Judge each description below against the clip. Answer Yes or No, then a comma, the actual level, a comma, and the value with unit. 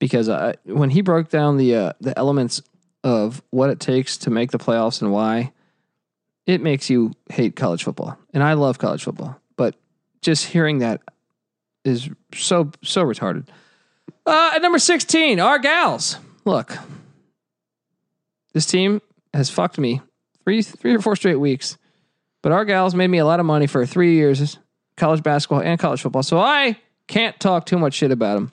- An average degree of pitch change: No, wide, 5.7 semitones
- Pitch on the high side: No, medium, 155 Hz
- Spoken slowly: No, average, 175 wpm